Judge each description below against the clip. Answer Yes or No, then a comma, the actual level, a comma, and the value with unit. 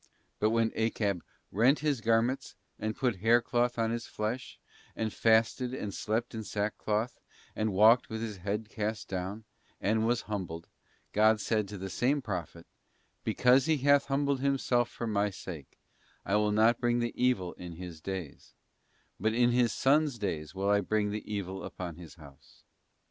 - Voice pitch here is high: No, low, 110 Hz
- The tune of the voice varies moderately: Yes, average, 3.3 semitones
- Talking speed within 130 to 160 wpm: No, average, 170 wpm